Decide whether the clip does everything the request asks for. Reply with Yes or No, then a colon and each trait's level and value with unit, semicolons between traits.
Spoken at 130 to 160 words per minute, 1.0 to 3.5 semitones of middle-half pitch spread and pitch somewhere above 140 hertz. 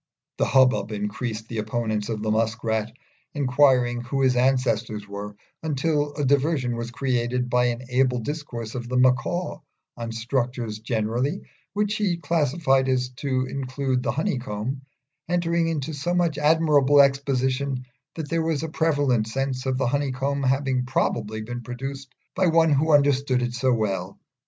No: average, 155 wpm; average, 3.2 semitones; low, 130 Hz